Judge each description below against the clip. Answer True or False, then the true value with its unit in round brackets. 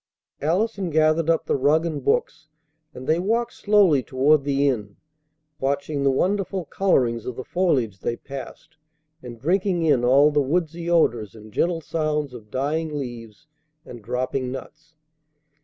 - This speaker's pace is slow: False (150 wpm)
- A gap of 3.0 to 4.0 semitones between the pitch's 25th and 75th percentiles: False (4.5 semitones)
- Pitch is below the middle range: False (145 Hz)